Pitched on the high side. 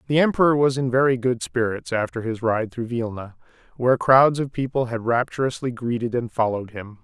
No: low, 120 Hz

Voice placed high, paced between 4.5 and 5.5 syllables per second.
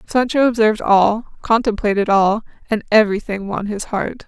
Yes: high, 215 Hz; 5.3 syllables/s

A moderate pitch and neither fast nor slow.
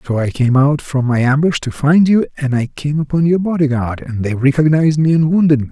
No: medium, 145 Hz; fast, 240 wpm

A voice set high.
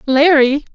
Yes: very high, 285 Hz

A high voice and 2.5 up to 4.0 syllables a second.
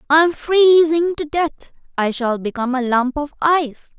No: very high, 290 Hz; 4.9 syllables/s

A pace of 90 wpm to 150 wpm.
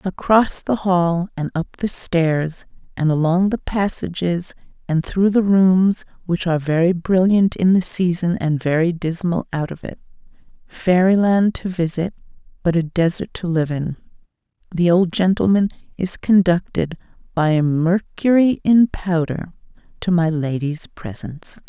Yes: average, 140 wpm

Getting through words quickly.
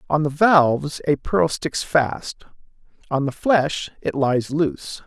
No: average, 155 wpm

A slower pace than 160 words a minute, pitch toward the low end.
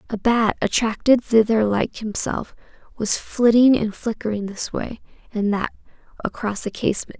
No: average, 140 wpm; high, 220 Hz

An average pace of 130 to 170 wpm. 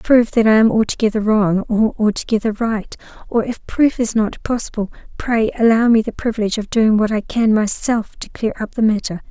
No: average, 200 wpm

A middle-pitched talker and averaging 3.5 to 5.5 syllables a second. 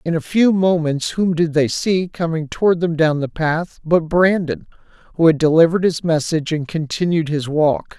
Yes: medium, 165 Hz; 4.9 syllables/s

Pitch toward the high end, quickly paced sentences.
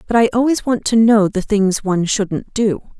Yes: high, 210 Hz; fast, 220 wpm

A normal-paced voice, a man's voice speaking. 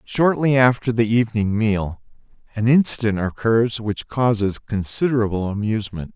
No: slow, 115 wpm; male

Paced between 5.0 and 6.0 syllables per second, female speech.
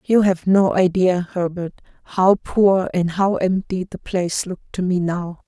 No: 4.4 syllables/s; female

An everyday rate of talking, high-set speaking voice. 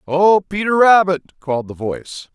No: average, 155 wpm; medium, 175 Hz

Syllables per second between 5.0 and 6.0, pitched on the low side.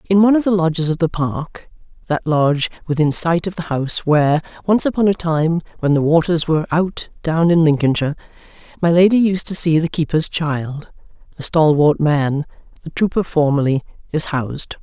No: 5.4 syllables/s; medium, 160 Hz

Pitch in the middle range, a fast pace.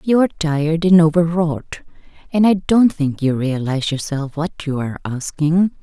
No: medium, 160 Hz; average, 165 wpm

